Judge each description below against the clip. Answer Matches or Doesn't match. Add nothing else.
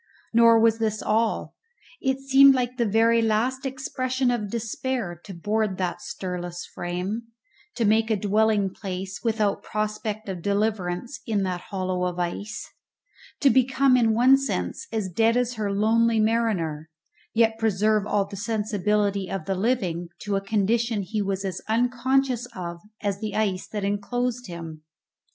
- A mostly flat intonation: Doesn't match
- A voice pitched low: Doesn't match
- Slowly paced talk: Doesn't match